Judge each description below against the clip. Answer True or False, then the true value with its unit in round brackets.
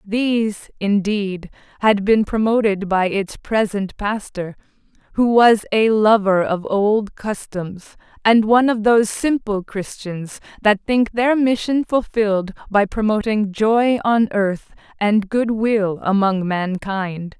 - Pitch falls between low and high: False (210 Hz)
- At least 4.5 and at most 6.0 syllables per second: False (3.7 syllables/s)